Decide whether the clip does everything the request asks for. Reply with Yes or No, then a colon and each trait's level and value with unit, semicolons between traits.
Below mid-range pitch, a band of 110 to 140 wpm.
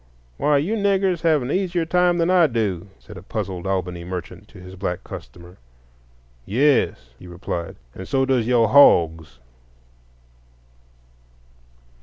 Yes: low, 110 Hz; slow, 135 wpm